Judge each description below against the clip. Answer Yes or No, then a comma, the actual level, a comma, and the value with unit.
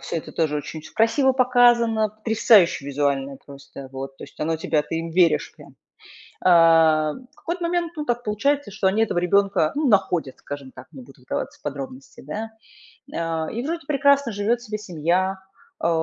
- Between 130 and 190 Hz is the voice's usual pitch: Yes, medium, 185 Hz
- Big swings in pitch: Yes, wide, 7.7 semitones